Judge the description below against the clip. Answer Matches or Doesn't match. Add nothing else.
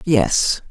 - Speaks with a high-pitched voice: Doesn't match